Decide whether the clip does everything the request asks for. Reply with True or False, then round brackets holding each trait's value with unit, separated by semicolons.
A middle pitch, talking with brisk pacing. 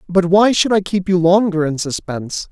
True (180 Hz; 215 wpm)